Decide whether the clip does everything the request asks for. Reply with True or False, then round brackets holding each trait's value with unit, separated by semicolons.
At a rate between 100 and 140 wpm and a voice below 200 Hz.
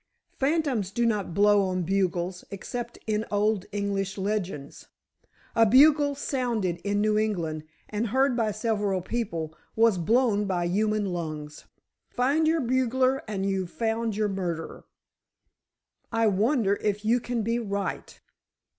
False (135 wpm; 210 Hz)